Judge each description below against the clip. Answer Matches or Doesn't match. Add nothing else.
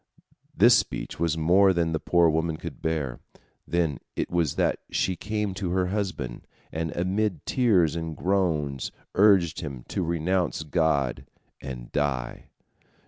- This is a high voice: Doesn't match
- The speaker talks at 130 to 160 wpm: Matches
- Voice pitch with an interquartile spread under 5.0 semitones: Matches